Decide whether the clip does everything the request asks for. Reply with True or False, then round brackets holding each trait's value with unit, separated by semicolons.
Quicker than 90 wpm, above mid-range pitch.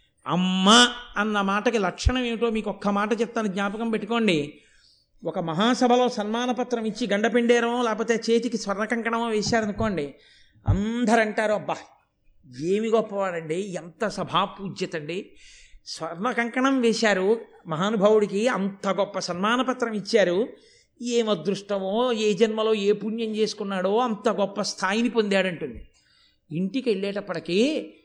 True (105 wpm; 215 Hz)